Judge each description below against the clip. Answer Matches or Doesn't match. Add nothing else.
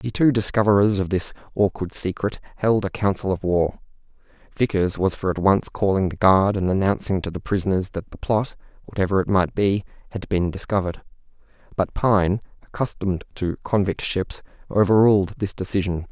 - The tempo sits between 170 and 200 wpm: Doesn't match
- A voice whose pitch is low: Matches